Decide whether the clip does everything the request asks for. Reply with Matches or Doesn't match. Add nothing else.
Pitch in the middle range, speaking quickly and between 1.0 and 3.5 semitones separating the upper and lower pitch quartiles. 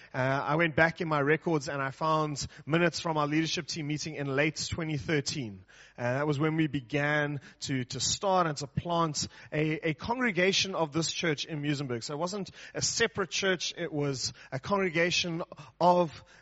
Doesn't match